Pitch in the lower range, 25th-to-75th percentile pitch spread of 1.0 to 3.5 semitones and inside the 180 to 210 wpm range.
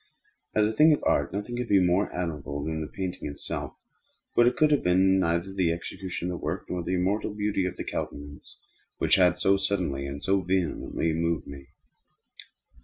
Yes: very low, 90 Hz; average, 3.0 semitones; average, 190 wpm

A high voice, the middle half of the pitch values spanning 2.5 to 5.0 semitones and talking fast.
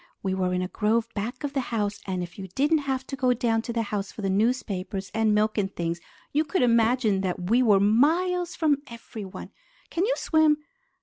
No: high, 225 Hz; wide, 5.5 semitones; fast, 210 wpm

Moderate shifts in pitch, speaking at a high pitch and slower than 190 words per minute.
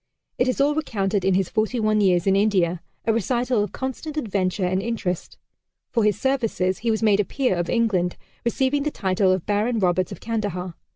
No: average, 4.2 semitones; high, 210 Hz; average, 195 wpm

